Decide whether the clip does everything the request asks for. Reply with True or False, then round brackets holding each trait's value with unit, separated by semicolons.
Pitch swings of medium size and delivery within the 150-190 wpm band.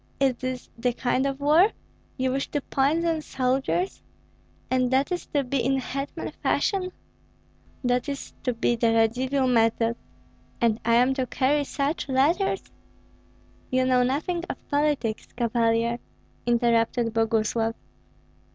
False (3.2 semitones; 135 wpm)